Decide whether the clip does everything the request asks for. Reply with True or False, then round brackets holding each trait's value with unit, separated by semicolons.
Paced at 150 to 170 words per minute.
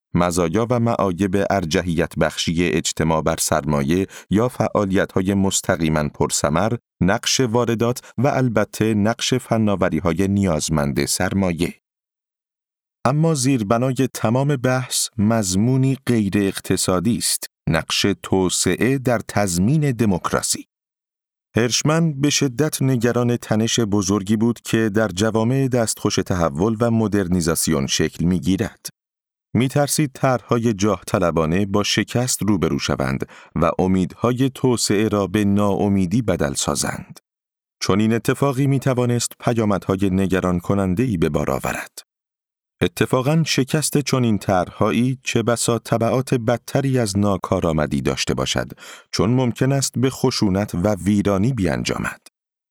False (115 wpm)